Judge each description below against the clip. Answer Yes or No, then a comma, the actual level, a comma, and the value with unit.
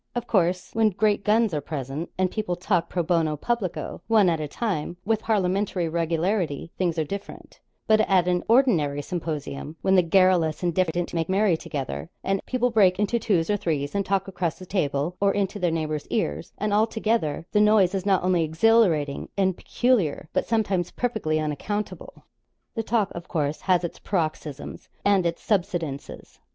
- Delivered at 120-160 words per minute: No, average, 175 wpm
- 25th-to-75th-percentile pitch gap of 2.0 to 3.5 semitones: No, average, 4.4 semitones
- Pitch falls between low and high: Yes, medium, 180 Hz